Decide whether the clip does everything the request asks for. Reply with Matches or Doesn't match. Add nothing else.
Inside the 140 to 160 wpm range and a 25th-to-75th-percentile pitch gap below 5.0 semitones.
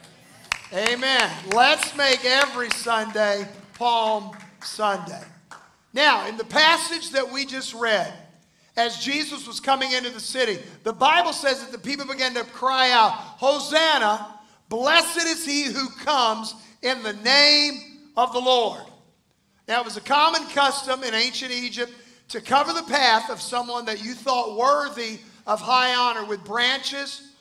Matches